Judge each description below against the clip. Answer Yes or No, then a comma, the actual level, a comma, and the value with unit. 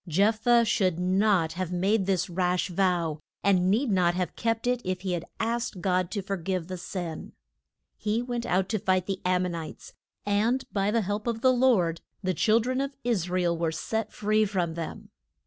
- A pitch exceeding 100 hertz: Yes, high, 190 Hz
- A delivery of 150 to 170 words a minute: No, fast, 205 wpm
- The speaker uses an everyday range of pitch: Yes, average, 3.7 semitones